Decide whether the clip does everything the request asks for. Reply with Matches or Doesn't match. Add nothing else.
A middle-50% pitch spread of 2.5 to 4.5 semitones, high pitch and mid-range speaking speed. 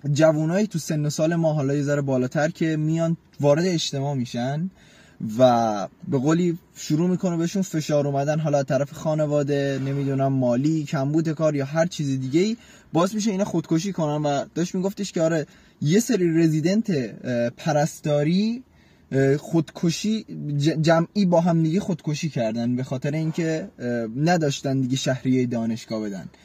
Doesn't match